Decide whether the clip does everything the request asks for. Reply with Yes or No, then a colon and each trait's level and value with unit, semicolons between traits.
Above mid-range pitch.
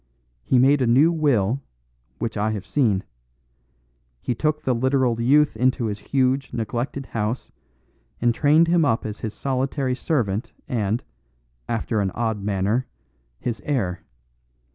No: low, 120 Hz